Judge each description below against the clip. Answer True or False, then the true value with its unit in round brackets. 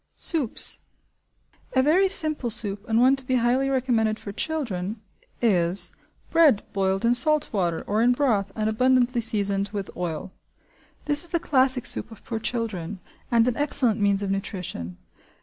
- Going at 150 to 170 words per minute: True (160 wpm)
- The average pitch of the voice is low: False (230 Hz)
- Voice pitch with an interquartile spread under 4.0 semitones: False (4.7 semitones)